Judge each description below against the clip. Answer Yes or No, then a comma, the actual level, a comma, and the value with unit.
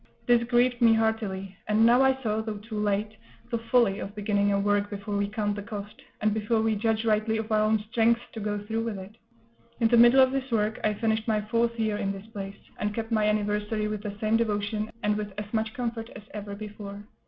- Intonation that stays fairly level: Yes, narrow, 1.6 semitones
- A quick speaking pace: Yes, fast, 230 wpm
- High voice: Yes, high, 215 Hz